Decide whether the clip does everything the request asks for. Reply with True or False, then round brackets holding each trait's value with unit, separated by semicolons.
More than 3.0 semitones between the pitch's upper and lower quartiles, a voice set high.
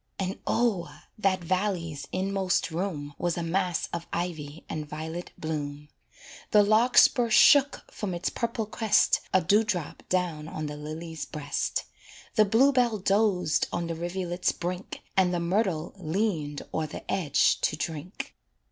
False (4.0 semitones; 180 Hz)